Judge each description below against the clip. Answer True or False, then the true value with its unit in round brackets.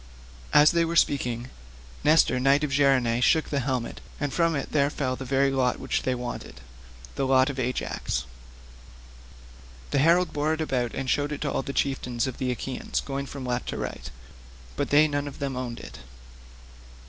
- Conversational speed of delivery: True (185 wpm)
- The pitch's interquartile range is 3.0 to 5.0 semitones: False (2.6 semitones)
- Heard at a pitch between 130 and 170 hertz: True (135 Hz)